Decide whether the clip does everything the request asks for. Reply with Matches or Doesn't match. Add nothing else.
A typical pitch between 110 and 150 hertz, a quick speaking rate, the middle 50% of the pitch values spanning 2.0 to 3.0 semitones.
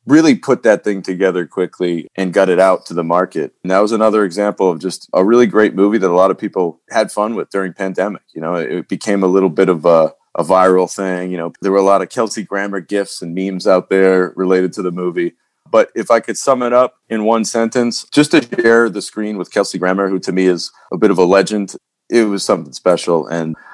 Doesn't match